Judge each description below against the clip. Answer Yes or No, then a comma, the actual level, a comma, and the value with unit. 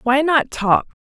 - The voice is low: No, very high, 270 Hz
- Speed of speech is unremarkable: Yes, average, 175 wpm